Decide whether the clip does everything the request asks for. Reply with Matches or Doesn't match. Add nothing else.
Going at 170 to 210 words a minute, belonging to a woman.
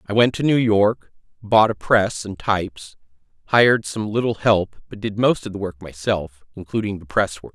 Doesn't match